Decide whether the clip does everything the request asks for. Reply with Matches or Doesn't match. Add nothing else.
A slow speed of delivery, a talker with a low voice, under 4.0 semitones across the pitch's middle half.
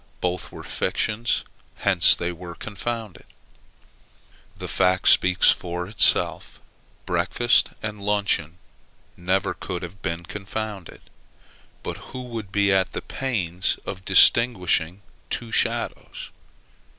Matches